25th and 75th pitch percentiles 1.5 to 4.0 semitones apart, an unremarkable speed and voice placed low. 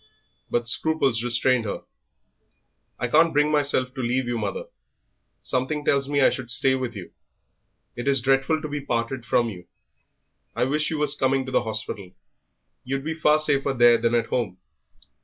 Yes: average, 3.4 semitones; average, 175 wpm; low, 130 Hz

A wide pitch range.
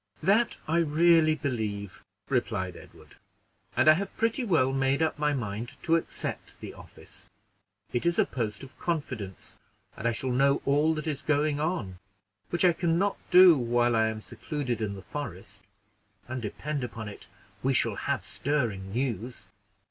Yes: wide, 5.7 semitones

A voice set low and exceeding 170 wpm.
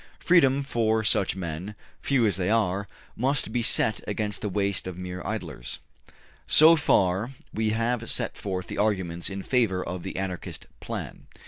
No: low, 105 Hz; average, 165 wpm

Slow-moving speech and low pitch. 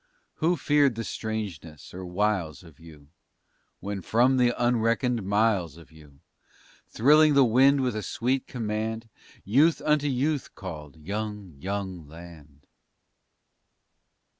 Yes: slow, 120 wpm; low, 105 Hz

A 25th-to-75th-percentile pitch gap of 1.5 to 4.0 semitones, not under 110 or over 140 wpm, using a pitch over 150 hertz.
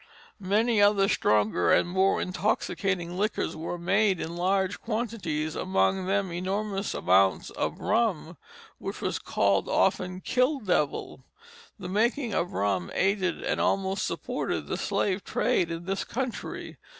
Yes: average, 3.3 semitones; slow, 135 wpm; high, 190 Hz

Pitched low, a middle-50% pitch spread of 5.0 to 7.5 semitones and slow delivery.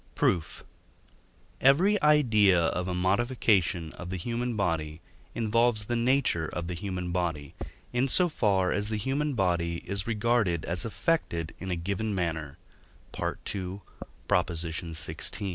Yes: very low, 95 Hz; wide, 5.5 semitones; slow, 130 wpm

